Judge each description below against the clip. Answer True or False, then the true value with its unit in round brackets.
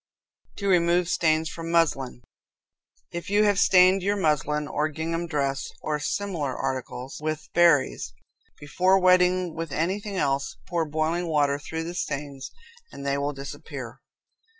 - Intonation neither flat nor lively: True (3.7 semitones)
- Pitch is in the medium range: True (160 Hz)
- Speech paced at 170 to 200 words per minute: False (140 wpm)